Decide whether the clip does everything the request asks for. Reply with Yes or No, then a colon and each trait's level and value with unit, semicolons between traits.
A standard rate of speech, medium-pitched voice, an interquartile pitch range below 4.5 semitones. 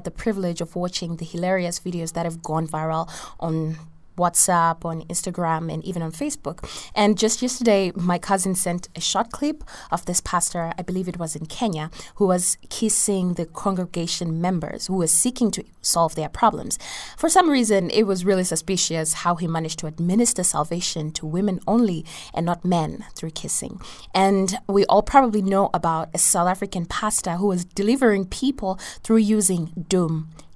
Yes: average, 175 wpm; medium, 180 Hz; average, 3.1 semitones